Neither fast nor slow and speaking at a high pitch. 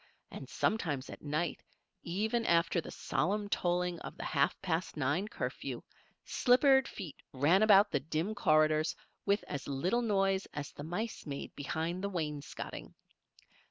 No: average, 145 wpm; medium, 175 Hz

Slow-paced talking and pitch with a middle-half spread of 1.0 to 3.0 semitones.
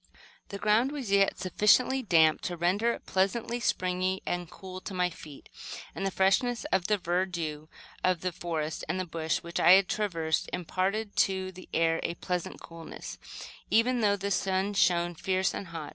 No: average, 170 wpm; average, 2.7 semitones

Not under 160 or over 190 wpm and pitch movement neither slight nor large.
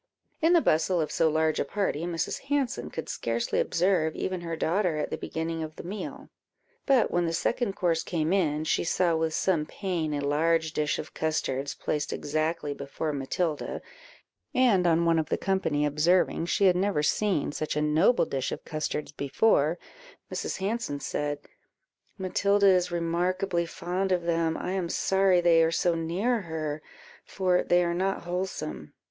Yes: average, 170 wpm; average, 3.2 semitones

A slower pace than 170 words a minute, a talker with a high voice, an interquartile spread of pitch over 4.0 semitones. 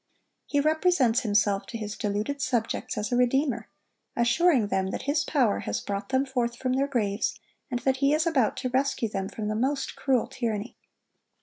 No: average, 185 wpm; high, 245 Hz; average, 4.4 semitones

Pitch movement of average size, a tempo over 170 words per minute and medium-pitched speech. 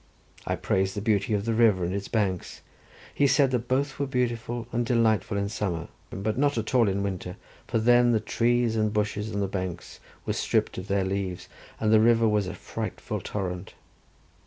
No: average, 3.2 semitones; average, 195 wpm; low, 110 Hz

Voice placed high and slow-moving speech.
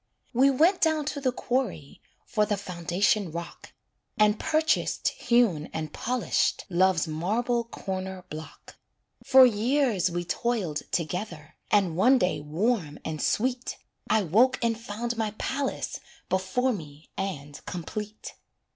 Yes: high, 205 Hz; slow, 130 wpm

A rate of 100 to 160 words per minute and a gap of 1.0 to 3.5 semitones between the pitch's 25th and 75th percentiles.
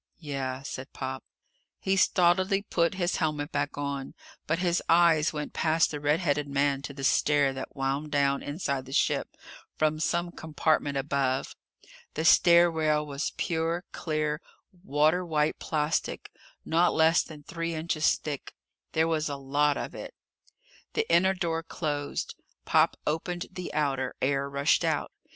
Yes: average, 150 wpm; average, 2.9 semitones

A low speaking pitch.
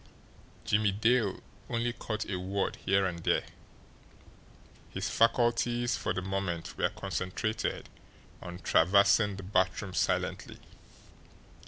Yes: low, 100 Hz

